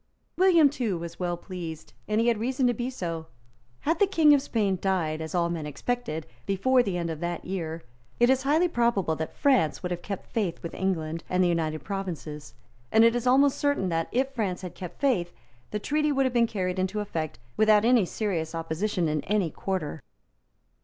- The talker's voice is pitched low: No, high, 195 Hz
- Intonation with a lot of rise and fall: Yes, wide, 6.4 semitones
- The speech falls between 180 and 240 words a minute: Yes, average, 200 wpm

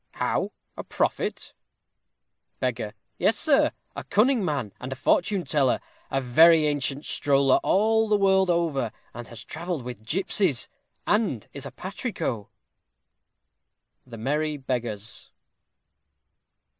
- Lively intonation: Yes, wide, 7.3 semitones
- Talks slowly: Yes, slow, 120 wpm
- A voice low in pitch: No, medium, 145 Hz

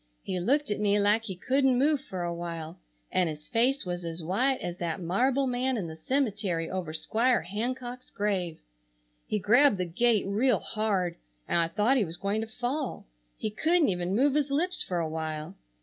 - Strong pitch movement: Yes, wide, 6.5 semitones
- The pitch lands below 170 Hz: No, high, 205 Hz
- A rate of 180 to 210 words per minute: Yes, average, 195 wpm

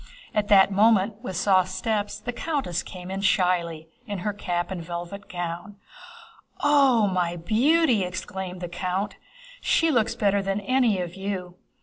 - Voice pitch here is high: Yes, high, 195 Hz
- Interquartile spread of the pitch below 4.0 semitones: Yes, average, 3.1 semitones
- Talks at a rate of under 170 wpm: Yes, average, 155 wpm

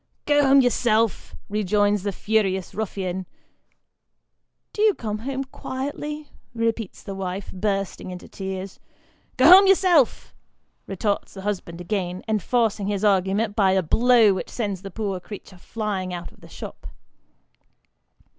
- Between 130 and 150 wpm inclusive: Yes, average, 140 wpm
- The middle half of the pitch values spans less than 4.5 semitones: Yes, average, 3.4 semitones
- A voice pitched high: Yes, high, 205 Hz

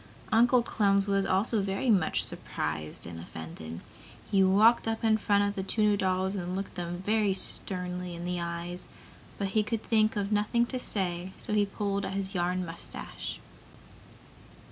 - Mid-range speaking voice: No, high, 195 Hz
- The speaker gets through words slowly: No, average, 165 wpm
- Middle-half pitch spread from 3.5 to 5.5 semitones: No, average, 2.9 semitones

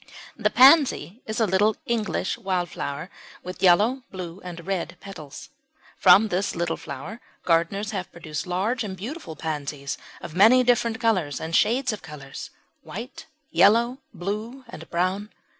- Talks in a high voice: Yes, high, 195 Hz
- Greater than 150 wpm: No, average, 145 wpm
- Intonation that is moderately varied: Yes, average, 4.9 semitones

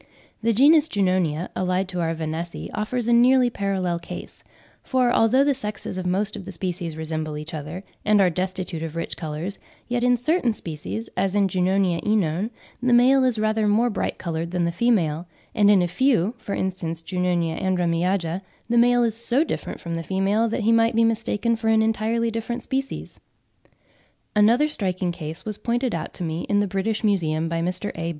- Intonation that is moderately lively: Yes, average, 5.0 semitones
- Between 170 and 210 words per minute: Yes, average, 190 wpm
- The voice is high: Yes, high, 195 Hz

